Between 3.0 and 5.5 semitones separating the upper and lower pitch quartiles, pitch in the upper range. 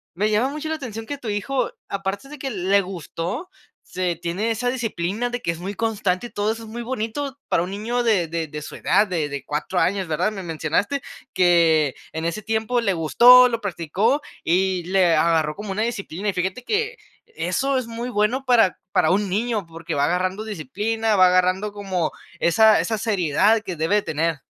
Yes: average, 4.8 semitones; high, 200 Hz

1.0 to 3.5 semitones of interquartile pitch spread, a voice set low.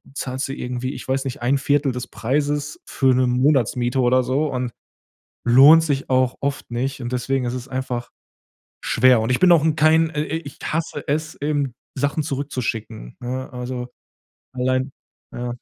Yes: narrow, 2.5 semitones; low, 130 Hz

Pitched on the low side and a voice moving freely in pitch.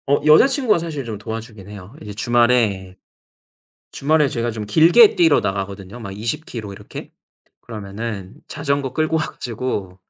Yes: low, 115 Hz; wide, 6.2 semitones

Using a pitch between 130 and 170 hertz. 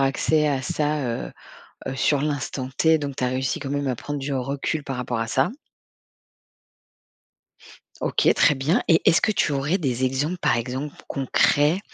Yes: medium, 140 Hz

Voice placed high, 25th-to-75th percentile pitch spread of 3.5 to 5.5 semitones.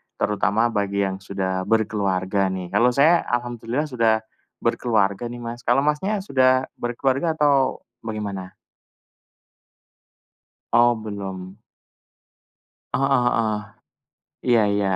No: low, 115 Hz; average, 4.0 semitones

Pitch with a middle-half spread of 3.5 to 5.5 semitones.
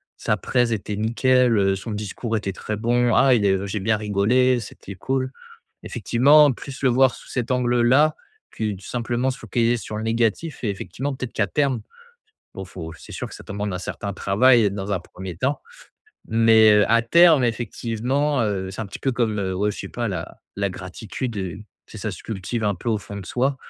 Yes: average, 3.9 semitones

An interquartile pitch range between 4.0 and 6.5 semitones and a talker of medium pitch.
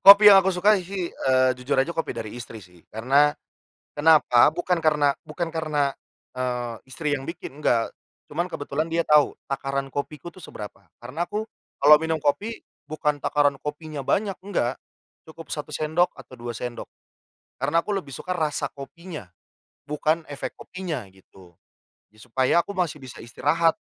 Yes: average, 4.4 semitones; medium, 150 Hz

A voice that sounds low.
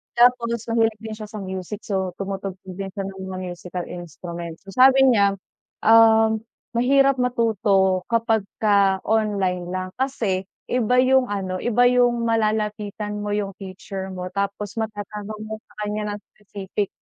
No: high, 210 Hz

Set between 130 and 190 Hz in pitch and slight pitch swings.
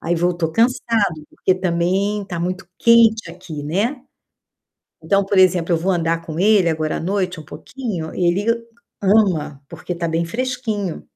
No: medium, 185 Hz; average, 3.7 semitones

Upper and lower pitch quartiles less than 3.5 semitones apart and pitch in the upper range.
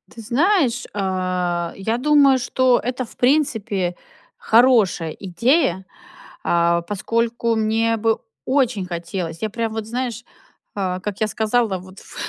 No: average, 4.6 semitones; high, 220 Hz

